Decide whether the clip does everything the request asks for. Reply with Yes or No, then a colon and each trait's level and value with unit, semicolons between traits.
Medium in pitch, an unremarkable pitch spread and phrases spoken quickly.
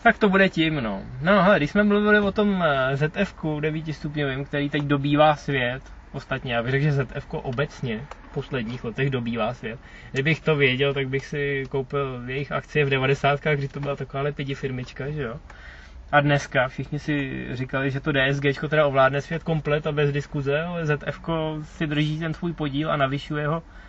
No: medium, 145 Hz; narrow, 2.2 semitones; fast, 190 wpm